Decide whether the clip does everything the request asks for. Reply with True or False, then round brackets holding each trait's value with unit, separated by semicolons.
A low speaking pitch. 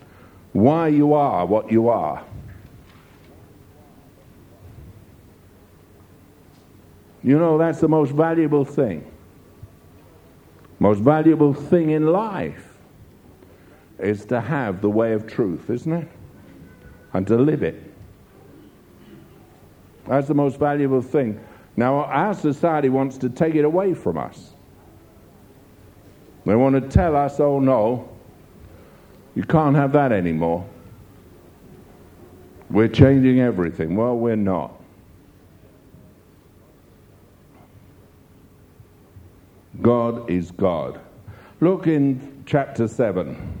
True (115 Hz)